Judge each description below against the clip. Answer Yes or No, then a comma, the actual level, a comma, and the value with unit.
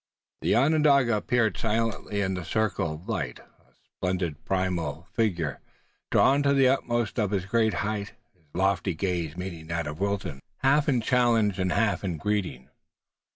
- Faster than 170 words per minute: No, average, 155 wpm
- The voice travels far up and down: No, average, 4.8 semitones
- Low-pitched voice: Yes, low, 100 Hz